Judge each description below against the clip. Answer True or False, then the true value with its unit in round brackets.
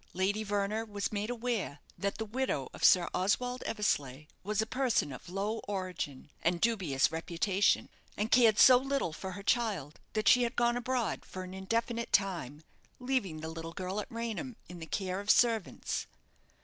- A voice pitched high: True (205 Hz)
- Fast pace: False (175 wpm)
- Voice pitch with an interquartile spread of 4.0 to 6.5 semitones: True (4.5 semitones)